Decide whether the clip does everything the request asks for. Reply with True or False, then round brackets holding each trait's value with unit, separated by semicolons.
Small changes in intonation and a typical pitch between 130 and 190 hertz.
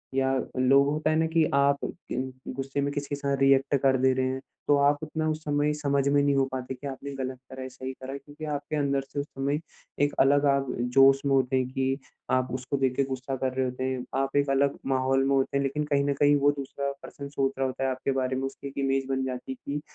True (1.3 semitones; 135 Hz)